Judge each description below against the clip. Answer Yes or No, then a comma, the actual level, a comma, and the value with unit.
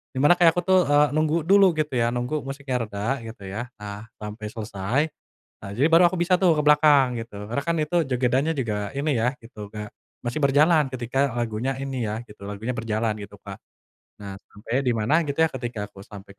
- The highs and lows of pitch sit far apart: Yes, wide, 5.9 semitones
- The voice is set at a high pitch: No, low, 125 Hz